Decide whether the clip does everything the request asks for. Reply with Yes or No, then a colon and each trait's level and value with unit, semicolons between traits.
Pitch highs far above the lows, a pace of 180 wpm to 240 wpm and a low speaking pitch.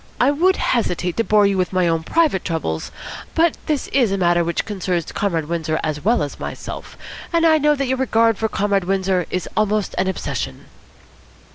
No: wide, 6.2 semitones; average, 190 wpm; high, 195 Hz